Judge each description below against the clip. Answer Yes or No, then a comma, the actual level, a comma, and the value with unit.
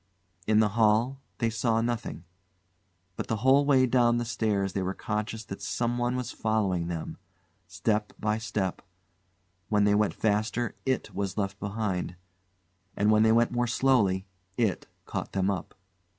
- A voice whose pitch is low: Yes, low, 110 Hz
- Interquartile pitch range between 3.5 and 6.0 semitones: No, average, 2.8 semitones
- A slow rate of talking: No, average, 150 wpm